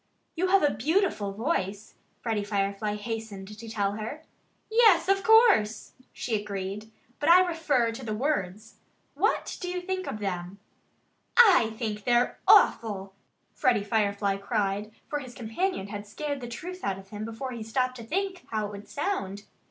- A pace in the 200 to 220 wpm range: No, average, 165 wpm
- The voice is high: Yes, high, 225 Hz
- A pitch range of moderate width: No, wide, 6.9 semitones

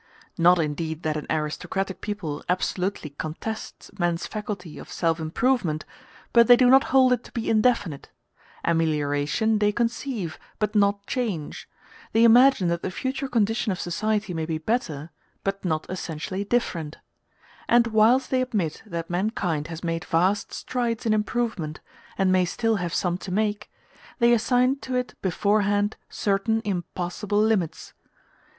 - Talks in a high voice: Yes, high, 200 Hz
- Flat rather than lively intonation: No, average, 5.3 semitones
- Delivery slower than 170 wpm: Yes, average, 145 wpm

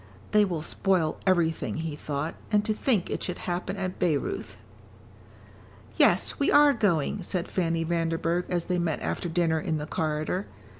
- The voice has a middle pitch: Yes, medium, 170 Hz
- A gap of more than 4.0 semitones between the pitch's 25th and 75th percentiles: No, average, 2.7 semitones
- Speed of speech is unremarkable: Yes, average, 160 wpm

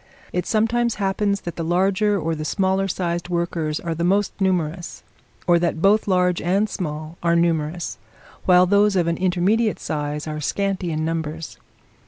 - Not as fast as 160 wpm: No, average, 165 wpm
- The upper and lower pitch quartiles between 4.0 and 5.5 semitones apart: No, average, 3.0 semitones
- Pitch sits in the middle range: Yes, medium, 175 Hz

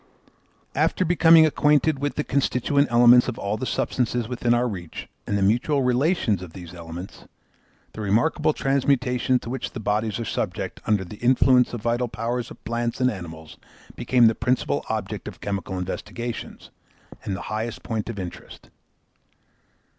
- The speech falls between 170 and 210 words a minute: No, average, 160 wpm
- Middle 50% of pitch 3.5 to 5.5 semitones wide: Yes, average, 3.9 semitones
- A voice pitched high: No, low, 120 Hz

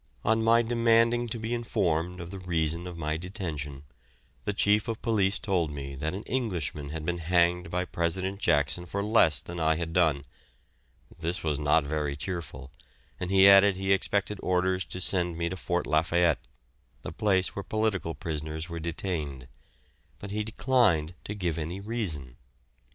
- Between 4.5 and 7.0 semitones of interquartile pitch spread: No, average, 4.0 semitones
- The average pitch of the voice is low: Yes, very low, 90 Hz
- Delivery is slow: No, average, 165 wpm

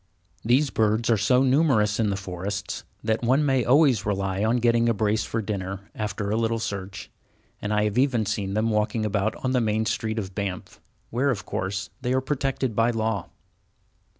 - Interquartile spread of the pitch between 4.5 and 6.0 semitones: No, average, 3.1 semitones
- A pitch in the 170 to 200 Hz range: No, low, 110 Hz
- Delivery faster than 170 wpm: Yes, average, 190 wpm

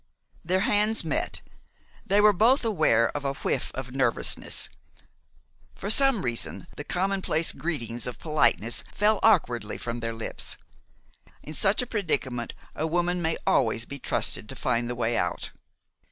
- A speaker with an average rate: Yes, average, 150 wpm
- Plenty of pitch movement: Yes, wide, 8.6 semitones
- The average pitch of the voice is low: No, medium, 155 Hz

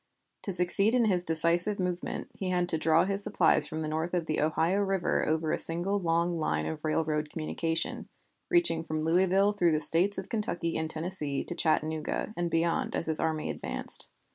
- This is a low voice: No, medium, 165 Hz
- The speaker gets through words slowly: No, average, 185 wpm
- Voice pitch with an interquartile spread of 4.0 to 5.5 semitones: No, average, 2.7 semitones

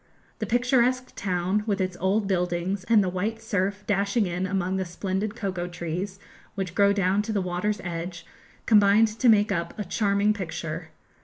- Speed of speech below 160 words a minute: No, average, 170 wpm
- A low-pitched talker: No, high, 195 Hz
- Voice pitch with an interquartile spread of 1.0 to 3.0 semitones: Yes, average, 2.7 semitones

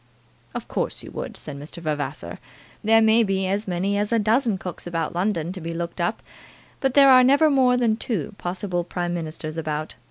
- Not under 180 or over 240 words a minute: Yes, average, 195 wpm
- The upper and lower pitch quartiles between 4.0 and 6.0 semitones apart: Yes, average, 5.1 semitones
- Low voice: No, medium, 185 Hz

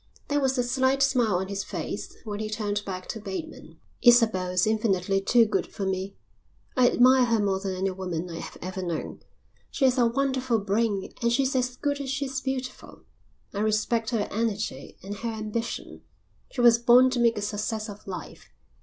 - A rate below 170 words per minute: No, average, 190 wpm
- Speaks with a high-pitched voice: Yes, high, 225 Hz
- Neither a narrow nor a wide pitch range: Yes, average, 4.1 semitones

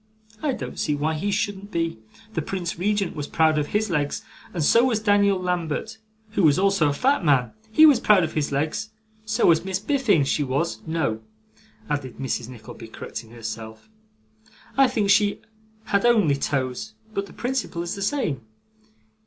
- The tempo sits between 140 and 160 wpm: No, average, 175 wpm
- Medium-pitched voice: Yes, medium, 175 Hz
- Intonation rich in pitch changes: Yes, wide, 6.4 semitones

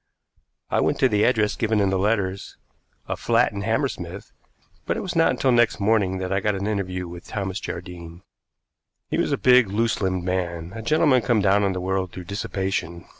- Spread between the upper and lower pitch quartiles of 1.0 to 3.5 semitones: Yes, average, 3.2 semitones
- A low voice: Yes, low, 100 Hz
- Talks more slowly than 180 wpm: No, average, 200 wpm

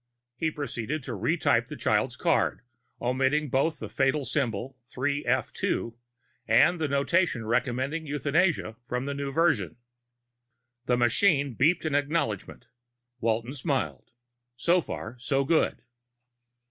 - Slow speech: Yes, slow, 120 wpm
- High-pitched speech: No, low, 135 Hz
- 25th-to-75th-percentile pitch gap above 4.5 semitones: No, average, 4.1 semitones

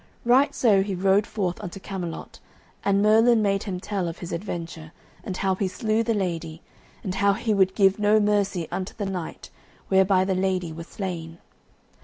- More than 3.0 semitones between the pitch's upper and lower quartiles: No, narrow, 2.4 semitones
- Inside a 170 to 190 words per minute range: Yes, average, 180 wpm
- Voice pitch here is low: No, high, 195 Hz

